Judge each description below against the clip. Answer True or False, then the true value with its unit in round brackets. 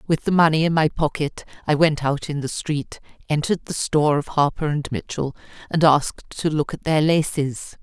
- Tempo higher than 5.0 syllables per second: True (5.2 syllables/s)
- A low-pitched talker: False (150 Hz)